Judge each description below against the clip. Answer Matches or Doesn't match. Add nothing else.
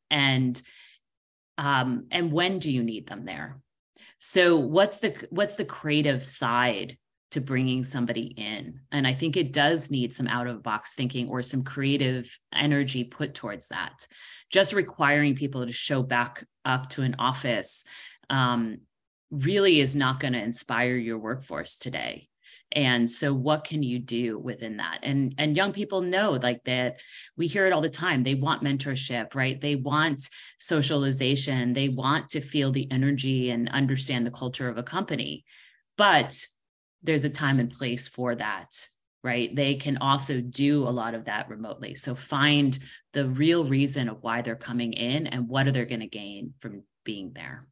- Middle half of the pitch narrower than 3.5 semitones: Matches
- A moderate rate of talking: Matches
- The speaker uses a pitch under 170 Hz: Matches